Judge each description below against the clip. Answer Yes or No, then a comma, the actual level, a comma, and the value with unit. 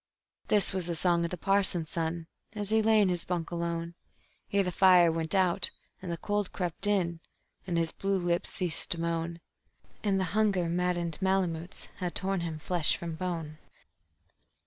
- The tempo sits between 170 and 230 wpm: Yes, average, 175 wpm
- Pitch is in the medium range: Yes, medium, 175 Hz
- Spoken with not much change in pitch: Yes, narrow, 2.3 semitones